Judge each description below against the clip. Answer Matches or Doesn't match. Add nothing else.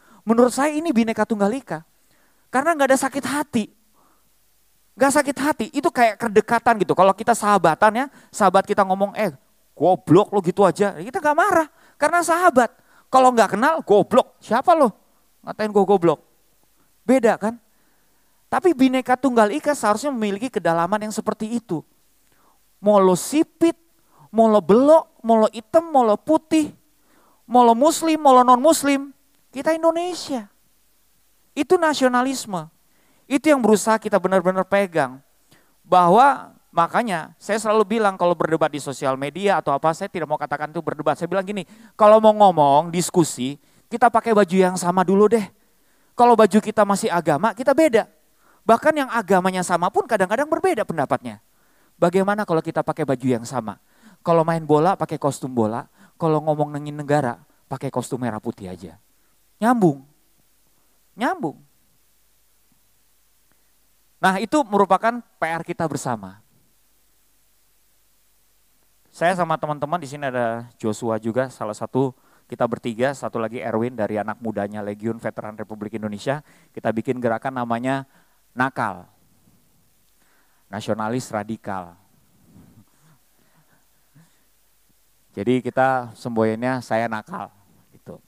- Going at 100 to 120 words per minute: Doesn't match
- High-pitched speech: Matches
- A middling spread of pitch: Doesn't match